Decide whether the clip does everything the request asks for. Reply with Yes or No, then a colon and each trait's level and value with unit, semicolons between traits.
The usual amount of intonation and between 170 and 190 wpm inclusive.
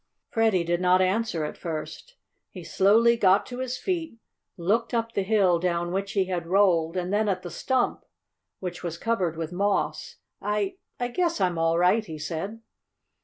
Yes: average, 4.6 semitones; average, 175 wpm